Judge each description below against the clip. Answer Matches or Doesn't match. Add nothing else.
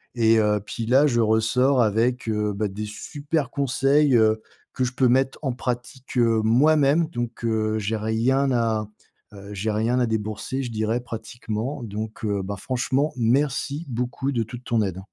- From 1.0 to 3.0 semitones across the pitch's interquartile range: Doesn't match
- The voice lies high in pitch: Doesn't match